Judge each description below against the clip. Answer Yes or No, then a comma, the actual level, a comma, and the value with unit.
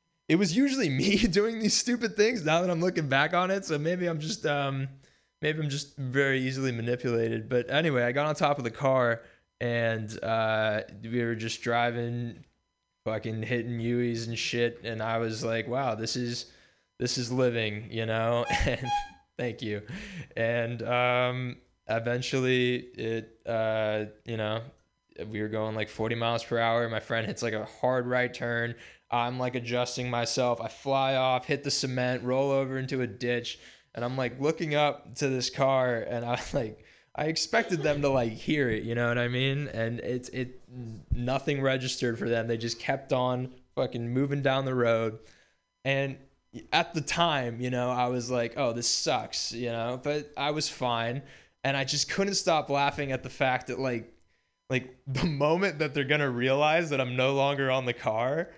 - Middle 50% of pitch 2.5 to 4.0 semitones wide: Yes, average, 3.2 semitones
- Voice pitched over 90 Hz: Yes, low, 125 Hz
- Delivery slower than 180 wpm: No, average, 185 wpm